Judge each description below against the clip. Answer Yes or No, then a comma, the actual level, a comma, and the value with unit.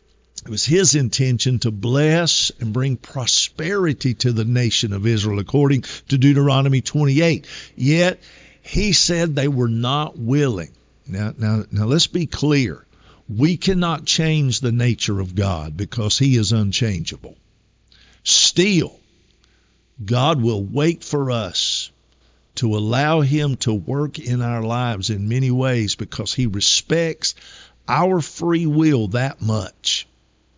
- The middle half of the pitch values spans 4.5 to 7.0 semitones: Yes, wide, 5.4 semitones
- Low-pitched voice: Yes, low, 125 Hz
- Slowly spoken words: Yes, slow, 130 wpm